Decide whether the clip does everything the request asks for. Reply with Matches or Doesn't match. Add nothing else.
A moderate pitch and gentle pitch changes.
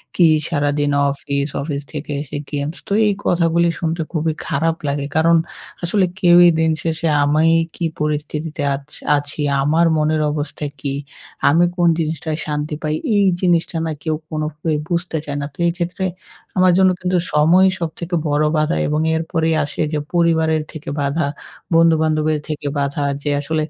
Matches